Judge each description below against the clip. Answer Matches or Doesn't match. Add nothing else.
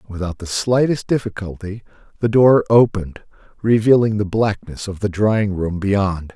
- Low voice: Matches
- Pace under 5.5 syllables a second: Matches